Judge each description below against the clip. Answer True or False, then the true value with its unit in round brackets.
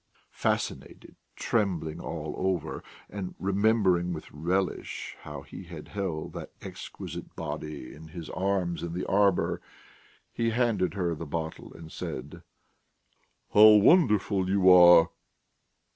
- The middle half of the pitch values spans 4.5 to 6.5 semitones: False (3.5 semitones)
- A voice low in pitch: True (90 Hz)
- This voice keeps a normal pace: False (120 wpm)